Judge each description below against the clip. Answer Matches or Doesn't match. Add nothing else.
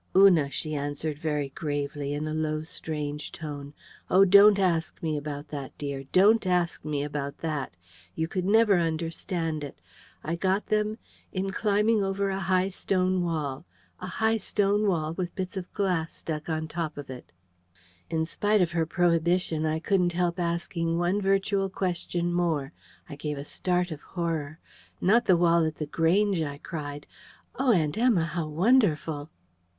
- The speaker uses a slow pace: Doesn't match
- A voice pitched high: Doesn't match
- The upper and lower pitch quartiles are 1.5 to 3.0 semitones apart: Doesn't match